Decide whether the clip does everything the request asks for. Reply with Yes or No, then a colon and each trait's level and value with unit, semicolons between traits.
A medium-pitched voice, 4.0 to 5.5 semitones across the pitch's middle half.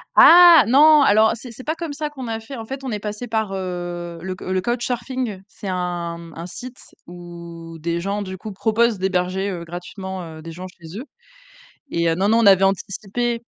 No: high, 195 Hz; average, 5.1 semitones